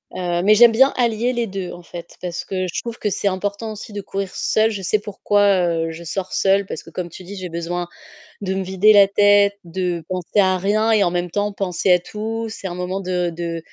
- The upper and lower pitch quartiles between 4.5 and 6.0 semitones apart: No, average, 2.7 semitones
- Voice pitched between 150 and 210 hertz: Yes, high, 190 Hz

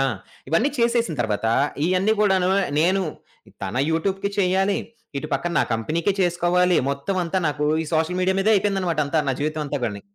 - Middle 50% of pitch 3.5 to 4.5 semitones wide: Yes, average, 3.9 semitones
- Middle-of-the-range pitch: Yes, medium, 180 Hz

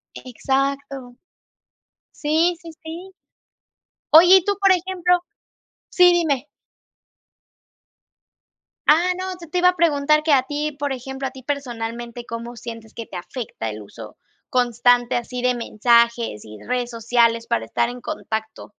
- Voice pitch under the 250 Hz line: No, very high, 255 Hz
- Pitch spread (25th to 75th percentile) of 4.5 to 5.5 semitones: Yes, average, 5.1 semitones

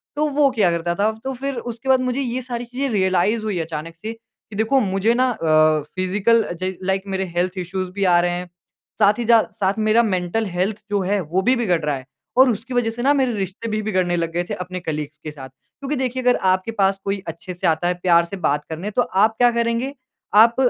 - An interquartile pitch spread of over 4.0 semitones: Yes, average, 4.9 semitones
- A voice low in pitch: No, high, 200 Hz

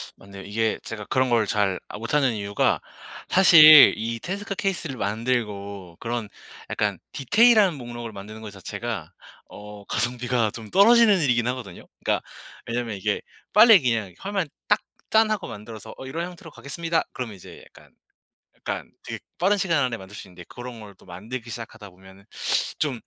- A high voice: No, low, 120 Hz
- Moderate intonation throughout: No, wide, 7.2 semitones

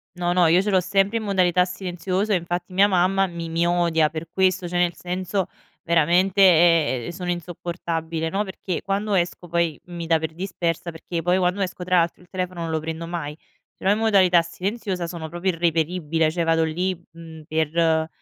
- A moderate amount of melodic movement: No, narrow, 2.0 semitones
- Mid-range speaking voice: Yes, medium, 175 Hz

